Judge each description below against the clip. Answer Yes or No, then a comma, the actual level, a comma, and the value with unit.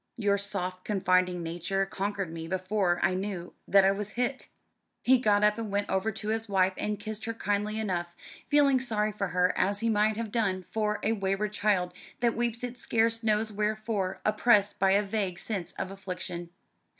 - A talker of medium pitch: No, high, 205 Hz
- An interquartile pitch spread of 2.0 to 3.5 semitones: Yes, narrow, 2.5 semitones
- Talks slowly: No, average, 185 wpm